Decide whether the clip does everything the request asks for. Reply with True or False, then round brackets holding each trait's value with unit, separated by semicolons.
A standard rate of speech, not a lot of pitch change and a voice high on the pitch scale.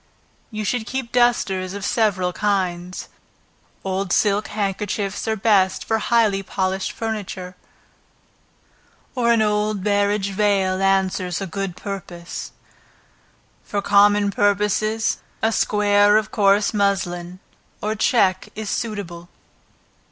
False (110 wpm; 2.0 semitones; 200 Hz)